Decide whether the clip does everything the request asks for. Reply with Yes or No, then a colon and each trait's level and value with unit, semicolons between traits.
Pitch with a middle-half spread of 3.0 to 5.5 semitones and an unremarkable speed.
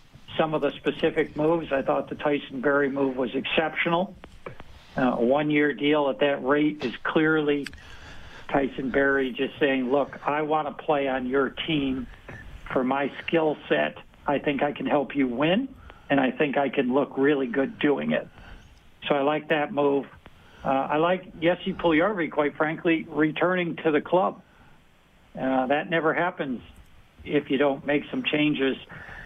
No: narrow, 2.4 semitones; average, 165 wpm